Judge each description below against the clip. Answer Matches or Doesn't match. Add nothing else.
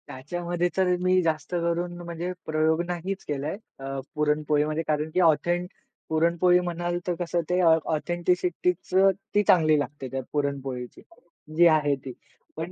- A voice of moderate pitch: Matches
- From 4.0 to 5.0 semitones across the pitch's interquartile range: Doesn't match